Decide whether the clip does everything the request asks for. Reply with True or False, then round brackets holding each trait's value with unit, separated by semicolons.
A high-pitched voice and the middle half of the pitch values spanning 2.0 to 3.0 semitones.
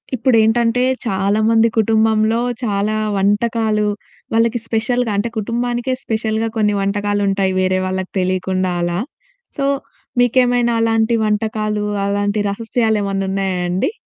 True (215 Hz; 2.5 semitones)